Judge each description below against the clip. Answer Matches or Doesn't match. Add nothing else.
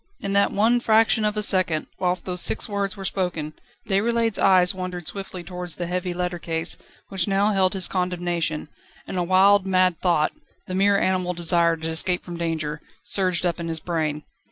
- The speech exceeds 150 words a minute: Matches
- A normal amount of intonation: Doesn't match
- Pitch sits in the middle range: Matches